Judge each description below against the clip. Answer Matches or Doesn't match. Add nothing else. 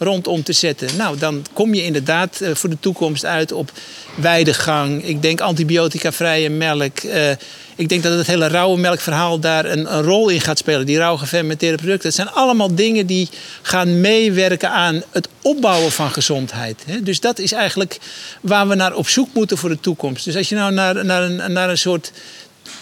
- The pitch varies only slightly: Doesn't match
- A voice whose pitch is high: Doesn't match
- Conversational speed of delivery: Matches